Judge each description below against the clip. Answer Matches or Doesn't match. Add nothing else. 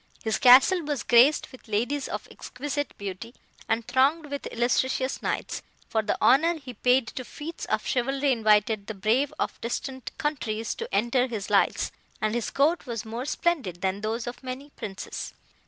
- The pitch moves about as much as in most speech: Matches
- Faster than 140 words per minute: Matches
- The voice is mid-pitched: Doesn't match